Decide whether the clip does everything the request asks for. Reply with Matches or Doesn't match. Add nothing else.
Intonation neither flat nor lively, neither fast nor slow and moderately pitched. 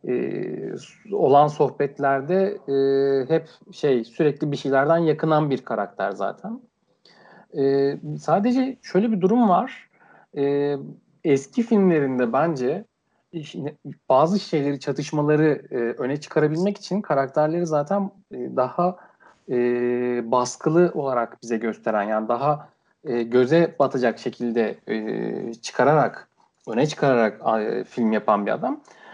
Matches